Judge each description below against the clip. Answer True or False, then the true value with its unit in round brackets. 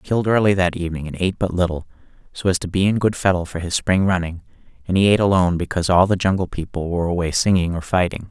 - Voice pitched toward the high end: False (90 Hz)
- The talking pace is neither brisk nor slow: False (245 wpm)